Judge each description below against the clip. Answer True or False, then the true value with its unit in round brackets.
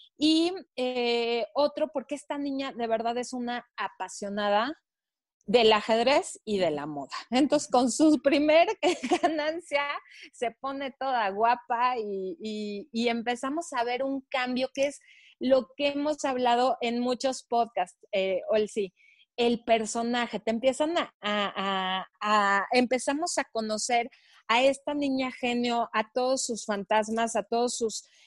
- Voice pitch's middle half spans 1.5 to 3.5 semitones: False (4.1 semitones)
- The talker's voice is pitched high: True (245 Hz)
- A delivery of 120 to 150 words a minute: True (145 wpm)